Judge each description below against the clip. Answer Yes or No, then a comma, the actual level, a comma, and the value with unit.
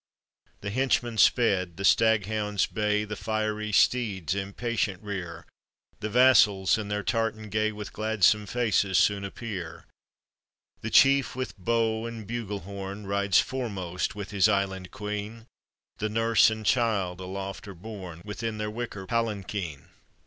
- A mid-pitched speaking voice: No, low, 105 Hz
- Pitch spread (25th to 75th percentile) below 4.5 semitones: Yes, narrow, 2.4 semitones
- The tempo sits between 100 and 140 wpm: Yes, slow, 135 wpm